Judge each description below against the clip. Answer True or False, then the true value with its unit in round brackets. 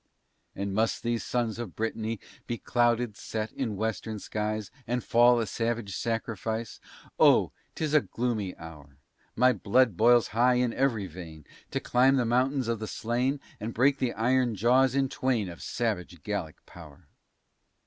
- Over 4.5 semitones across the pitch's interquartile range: False (2.9 semitones)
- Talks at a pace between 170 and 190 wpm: False (160 wpm)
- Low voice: True (115 Hz)